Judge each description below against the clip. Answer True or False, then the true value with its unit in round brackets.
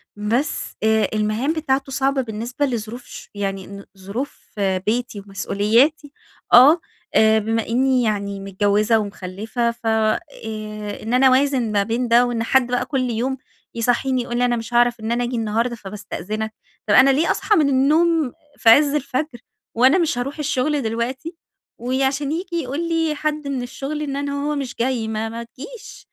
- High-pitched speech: True (245 Hz)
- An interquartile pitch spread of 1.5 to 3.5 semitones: False (3.9 semitones)